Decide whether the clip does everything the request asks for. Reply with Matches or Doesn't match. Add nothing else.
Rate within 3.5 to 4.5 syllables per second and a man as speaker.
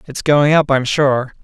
Matches